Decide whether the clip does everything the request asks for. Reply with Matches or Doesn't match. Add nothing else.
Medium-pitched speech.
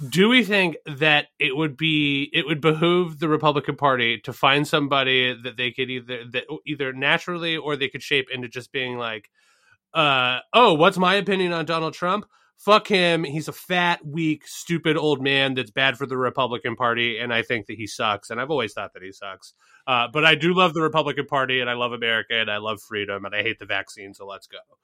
Matches